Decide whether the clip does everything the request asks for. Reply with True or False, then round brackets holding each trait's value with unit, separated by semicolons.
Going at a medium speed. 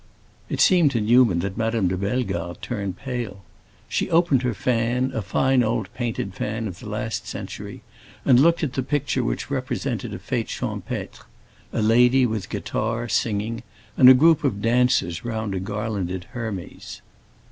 True (160 wpm)